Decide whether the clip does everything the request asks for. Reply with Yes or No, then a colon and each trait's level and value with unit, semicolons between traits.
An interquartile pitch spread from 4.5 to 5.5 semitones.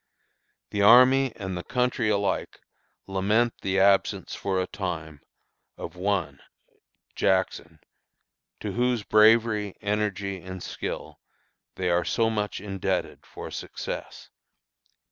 No: average, 2.8 semitones